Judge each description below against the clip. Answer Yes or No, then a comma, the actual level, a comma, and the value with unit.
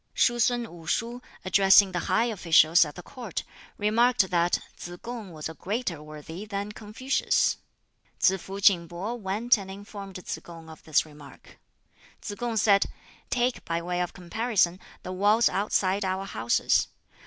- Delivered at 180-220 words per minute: No, average, 160 wpm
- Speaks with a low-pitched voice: No, high, 195 Hz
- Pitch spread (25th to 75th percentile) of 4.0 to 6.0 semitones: Yes, average, 4.3 semitones